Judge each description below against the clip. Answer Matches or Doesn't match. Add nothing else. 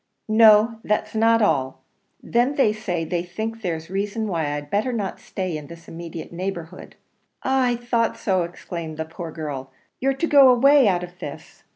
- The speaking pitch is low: Doesn't match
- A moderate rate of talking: Matches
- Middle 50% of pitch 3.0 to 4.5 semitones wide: Doesn't match